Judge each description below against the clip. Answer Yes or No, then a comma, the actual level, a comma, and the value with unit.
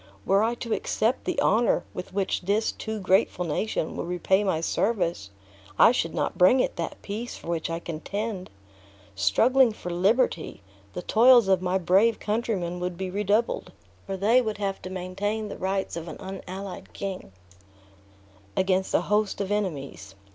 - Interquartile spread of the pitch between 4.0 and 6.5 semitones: No, average, 3.3 semitones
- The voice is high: Yes, high, 195 Hz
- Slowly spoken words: No, average, 165 wpm